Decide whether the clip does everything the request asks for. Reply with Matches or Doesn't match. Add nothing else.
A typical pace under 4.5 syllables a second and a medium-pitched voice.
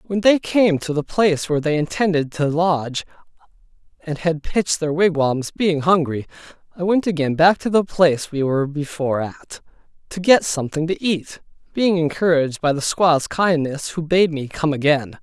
Doesn't match